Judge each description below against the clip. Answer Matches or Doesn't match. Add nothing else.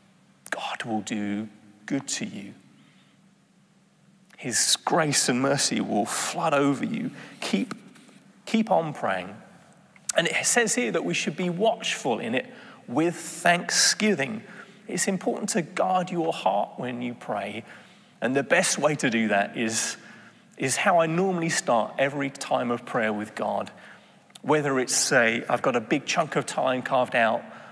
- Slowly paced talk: Doesn't match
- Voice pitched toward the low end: Doesn't match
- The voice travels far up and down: Matches